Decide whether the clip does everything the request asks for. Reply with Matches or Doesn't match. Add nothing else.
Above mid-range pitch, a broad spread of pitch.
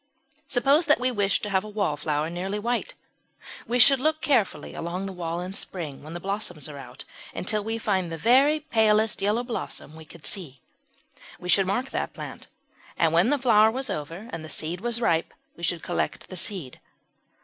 Matches